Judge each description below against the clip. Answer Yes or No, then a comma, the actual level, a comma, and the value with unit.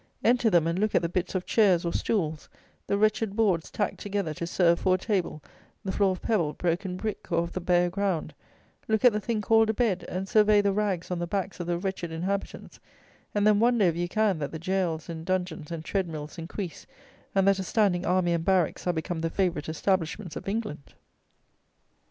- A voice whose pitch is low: No, medium, 185 Hz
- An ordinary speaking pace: No, fast, 215 wpm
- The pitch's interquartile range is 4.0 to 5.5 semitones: No, average, 3.3 semitones